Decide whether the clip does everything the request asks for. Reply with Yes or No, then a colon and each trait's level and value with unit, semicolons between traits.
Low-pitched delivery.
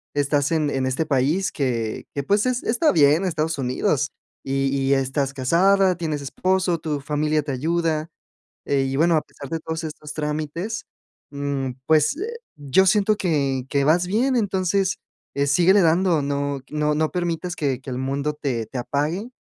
No: medium, 150 Hz